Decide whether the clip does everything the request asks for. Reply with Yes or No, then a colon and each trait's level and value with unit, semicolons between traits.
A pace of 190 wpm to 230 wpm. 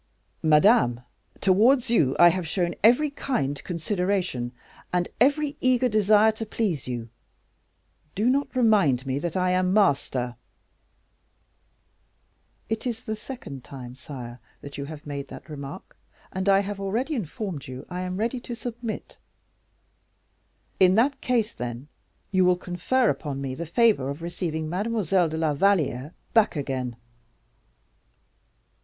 No: slow, 135 wpm